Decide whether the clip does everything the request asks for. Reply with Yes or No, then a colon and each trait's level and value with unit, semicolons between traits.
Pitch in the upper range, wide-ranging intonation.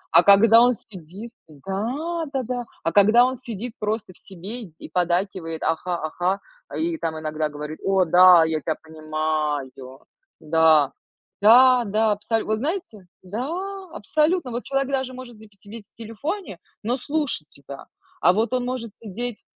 Yes: high, 215 Hz; wide, 6.7 semitones